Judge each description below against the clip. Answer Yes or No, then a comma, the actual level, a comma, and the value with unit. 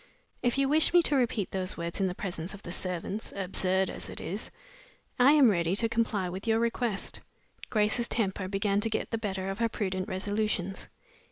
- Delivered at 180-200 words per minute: Yes, average, 195 wpm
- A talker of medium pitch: No, high, 200 Hz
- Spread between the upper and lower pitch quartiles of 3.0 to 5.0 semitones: Yes, average, 3.5 semitones